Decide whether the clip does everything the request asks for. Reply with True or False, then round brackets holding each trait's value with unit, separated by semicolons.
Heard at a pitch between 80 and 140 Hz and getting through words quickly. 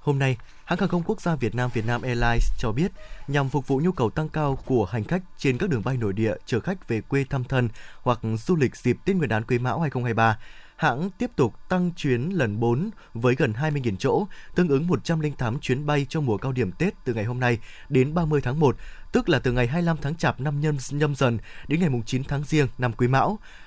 False (135 Hz; 235 wpm)